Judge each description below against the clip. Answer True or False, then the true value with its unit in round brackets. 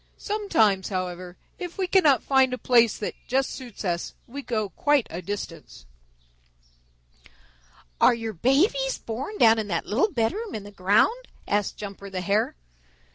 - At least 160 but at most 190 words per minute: False (150 wpm)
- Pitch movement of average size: False (5.7 semitones)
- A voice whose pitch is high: True (225 Hz)